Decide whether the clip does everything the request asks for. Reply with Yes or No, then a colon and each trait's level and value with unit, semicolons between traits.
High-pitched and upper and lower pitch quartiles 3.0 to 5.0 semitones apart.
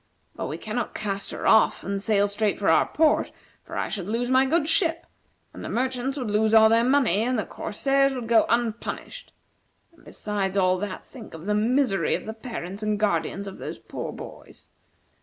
Yes: high, 220 Hz; average, 4.1 semitones